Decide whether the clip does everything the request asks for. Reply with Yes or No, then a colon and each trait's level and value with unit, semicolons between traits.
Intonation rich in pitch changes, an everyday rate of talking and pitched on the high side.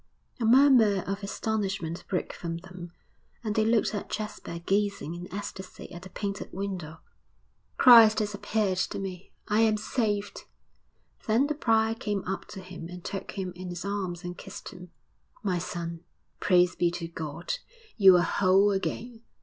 No: average, 3.2 semitones; average, 165 wpm; high, 195 Hz